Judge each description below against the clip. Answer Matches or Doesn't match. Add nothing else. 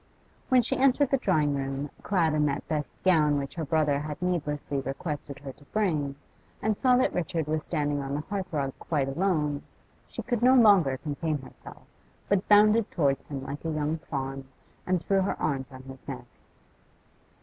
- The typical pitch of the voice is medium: Matches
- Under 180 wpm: Doesn't match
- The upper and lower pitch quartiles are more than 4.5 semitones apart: Matches